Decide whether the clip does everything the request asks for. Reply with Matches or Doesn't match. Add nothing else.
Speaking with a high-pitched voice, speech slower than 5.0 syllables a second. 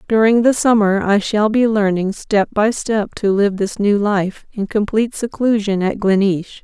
Matches